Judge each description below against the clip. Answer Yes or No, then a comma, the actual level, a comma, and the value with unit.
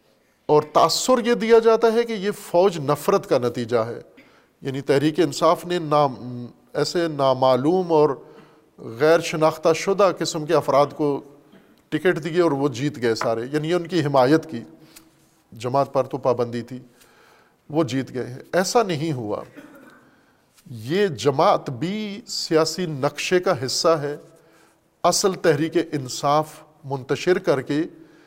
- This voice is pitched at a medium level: Yes, medium, 155 Hz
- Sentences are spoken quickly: No, average, 140 wpm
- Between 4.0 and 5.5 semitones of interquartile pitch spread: Yes, average, 4.3 semitones